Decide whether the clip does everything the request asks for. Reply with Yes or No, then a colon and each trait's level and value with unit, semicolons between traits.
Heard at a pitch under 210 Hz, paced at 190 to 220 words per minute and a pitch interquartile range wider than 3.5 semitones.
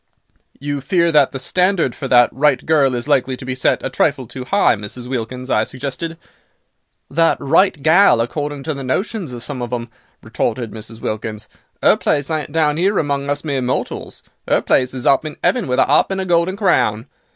Yes: medium, 140 Hz; average, 200 wpm; average, 4.3 semitones